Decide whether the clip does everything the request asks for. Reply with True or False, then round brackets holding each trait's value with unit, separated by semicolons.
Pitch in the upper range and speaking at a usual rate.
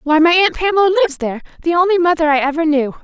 False (325 Hz; 235 wpm)